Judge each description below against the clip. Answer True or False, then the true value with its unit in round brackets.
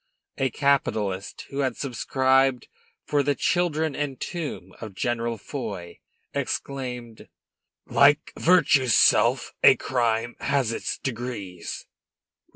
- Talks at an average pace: False (105 wpm)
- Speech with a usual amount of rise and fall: True (3.6 semitones)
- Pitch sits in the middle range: False (130 Hz)